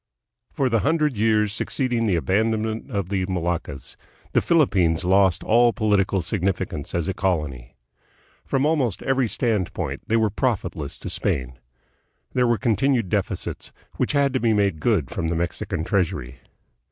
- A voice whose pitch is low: Yes, low, 100 Hz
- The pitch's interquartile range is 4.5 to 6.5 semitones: Yes, wide, 5.4 semitones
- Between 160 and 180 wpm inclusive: No, average, 150 wpm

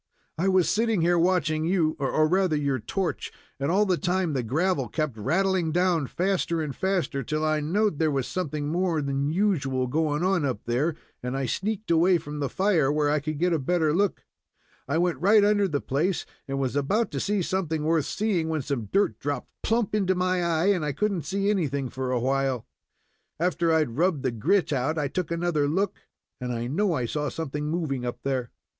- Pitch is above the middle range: No, medium, 160 Hz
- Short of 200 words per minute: No, fast, 205 wpm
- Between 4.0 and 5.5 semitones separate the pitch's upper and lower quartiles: Yes, average, 4.7 semitones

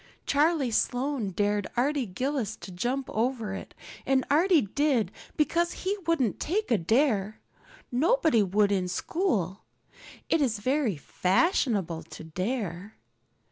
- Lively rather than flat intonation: Yes, wide, 6.6 semitones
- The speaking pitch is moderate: No, high, 240 Hz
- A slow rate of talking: Yes, slow, 125 wpm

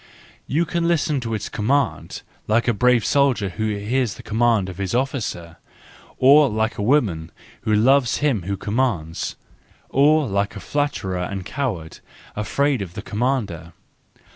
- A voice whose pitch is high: No, low, 115 Hz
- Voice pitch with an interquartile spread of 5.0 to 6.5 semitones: Yes, wide, 5.5 semitones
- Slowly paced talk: No, average, 150 wpm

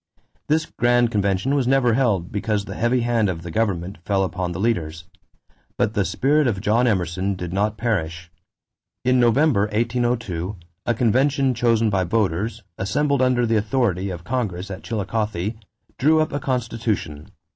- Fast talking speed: No, average, 155 wpm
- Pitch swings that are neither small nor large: Yes, average, 4.3 semitones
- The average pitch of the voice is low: Yes, low, 110 Hz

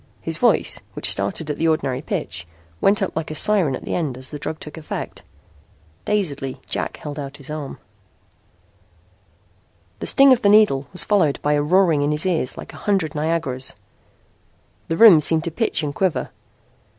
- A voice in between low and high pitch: Yes, medium, 155 Hz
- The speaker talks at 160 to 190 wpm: Yes, average, 180 wpm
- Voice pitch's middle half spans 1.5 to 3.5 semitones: No, average, 4.2 semitones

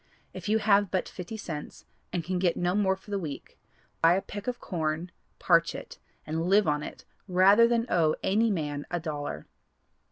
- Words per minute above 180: Yes, average, 190 wpm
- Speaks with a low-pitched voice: No, medium, 180 Hz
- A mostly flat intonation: No, average, 4.3 semitones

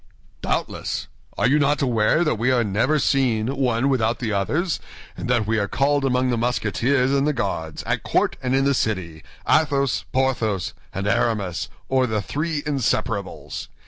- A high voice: No, low, 125 Hz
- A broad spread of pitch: No, average, 4.1 semitones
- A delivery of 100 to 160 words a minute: No, average, 170 wpm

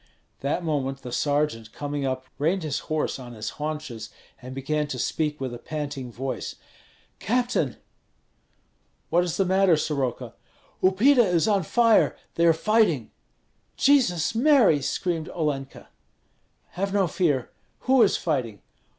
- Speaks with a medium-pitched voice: Yes, medium, 155 Hz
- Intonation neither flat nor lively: No, wide, 5.8 semitones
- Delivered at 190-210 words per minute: No, average, 140 wpm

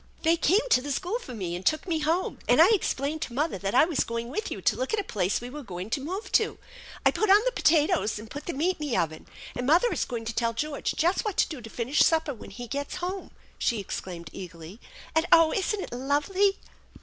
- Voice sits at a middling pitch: No, very high, 290 Hz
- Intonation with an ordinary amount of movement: No, wide, 7.2 semitones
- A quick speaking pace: Yes, fast, 255 wpm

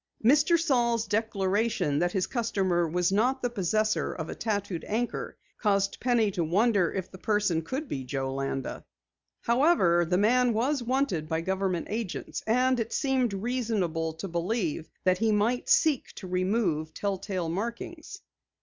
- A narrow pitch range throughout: No, average, 5.2 semitones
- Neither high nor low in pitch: No, high, 205 Hz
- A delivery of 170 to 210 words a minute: No, average, 160 wpm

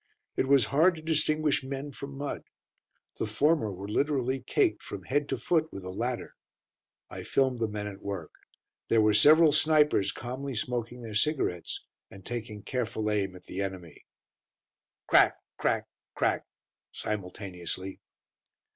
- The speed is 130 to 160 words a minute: Yes, average, 145 wpm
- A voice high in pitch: No, low, 120 Hz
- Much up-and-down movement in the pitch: Yes, wide, 5.8 semitones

